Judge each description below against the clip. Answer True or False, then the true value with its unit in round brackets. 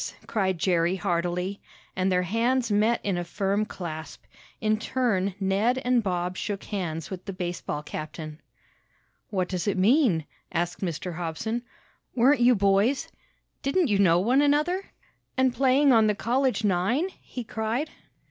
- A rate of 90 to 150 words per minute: True (145 wpm)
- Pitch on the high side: True (200 Hz)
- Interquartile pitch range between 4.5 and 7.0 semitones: True (5.3 semitones)